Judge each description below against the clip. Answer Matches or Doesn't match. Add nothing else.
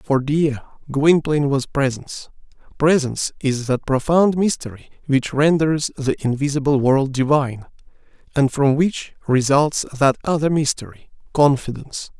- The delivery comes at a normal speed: Doesn't match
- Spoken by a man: Matches